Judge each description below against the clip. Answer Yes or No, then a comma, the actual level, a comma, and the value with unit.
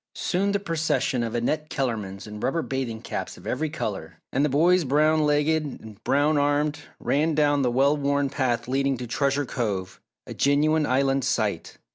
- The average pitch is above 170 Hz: No, medium, 140 Hz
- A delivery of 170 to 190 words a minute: Yes, average, 175 wpm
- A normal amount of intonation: Yes, average, 3.2 semitones